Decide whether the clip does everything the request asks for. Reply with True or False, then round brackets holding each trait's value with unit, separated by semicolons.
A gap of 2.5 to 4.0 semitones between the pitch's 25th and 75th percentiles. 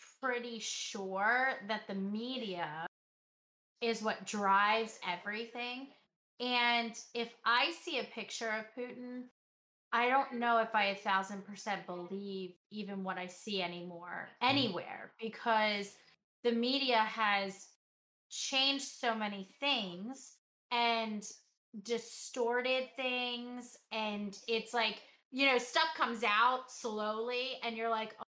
True (3.1 semitones)